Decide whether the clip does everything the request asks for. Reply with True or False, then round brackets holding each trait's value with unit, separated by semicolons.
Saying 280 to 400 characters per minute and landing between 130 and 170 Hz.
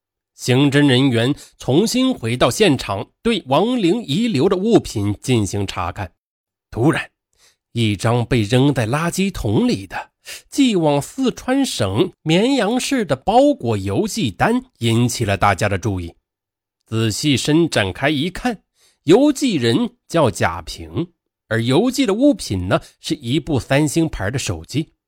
False (205 characters per minute; 140 Hz)